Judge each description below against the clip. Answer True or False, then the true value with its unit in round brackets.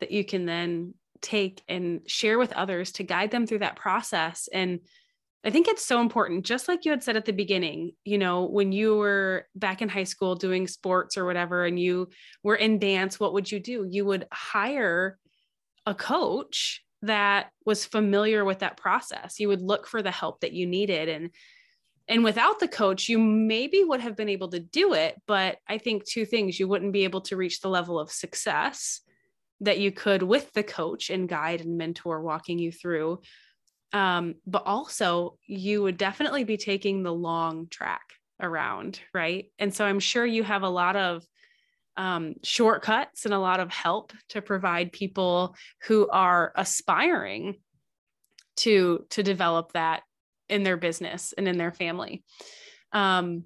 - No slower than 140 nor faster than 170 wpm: False (180 wpm)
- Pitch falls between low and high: False (195 Hz)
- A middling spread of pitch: True (3.2 semitones)